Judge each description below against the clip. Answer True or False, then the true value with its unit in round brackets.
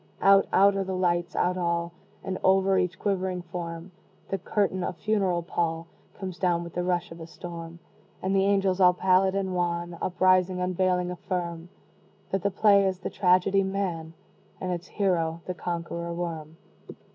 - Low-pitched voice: False (180 Hz)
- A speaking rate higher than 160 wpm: True (170 wpm)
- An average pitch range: False (1.9 semitones)